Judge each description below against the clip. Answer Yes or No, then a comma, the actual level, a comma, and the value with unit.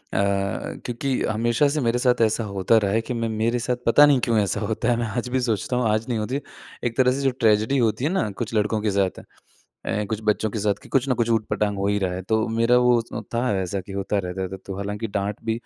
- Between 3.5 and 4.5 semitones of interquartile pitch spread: No, average, 3.0 semitones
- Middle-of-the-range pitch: No, low, 110 Hz